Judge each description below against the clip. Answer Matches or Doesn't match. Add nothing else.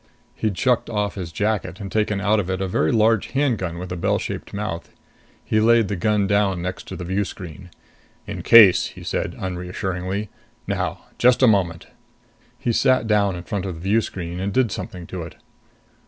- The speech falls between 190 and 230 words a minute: Matches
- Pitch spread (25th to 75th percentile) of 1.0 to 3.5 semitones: Matches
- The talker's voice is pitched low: Matches